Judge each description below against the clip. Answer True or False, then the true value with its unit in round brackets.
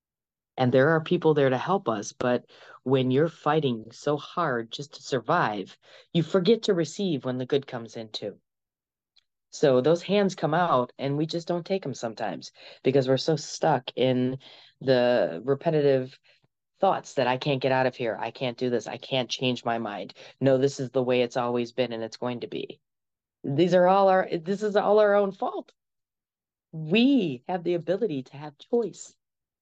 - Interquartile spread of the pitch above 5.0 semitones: True (5.5 semitones)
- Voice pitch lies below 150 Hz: True (140 Hz)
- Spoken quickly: False (190 wpm)